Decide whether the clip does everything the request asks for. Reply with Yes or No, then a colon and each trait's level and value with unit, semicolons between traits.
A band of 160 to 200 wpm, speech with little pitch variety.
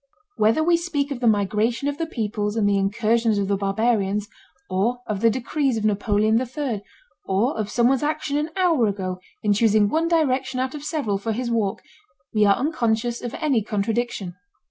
No: average, 185 wpm; average, 4.5 semitones